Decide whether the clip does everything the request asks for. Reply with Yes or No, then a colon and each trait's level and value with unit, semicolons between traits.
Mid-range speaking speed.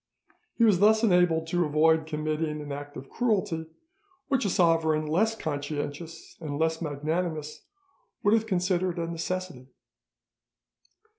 No: slow, 130 wpm